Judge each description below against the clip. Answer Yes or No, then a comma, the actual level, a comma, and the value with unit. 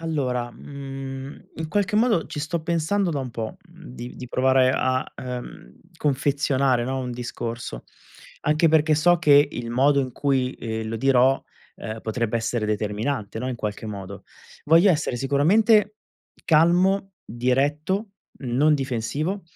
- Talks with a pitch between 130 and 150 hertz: Yes, low, 135 Hz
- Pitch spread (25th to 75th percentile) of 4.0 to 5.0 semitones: Yes, average, 4.7 semitones